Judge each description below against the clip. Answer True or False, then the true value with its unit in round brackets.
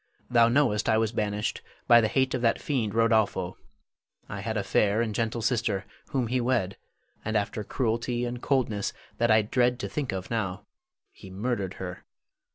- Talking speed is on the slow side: False (175 wpm)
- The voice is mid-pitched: False (110 Hz)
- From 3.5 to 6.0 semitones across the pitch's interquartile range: False (2.8 semitones)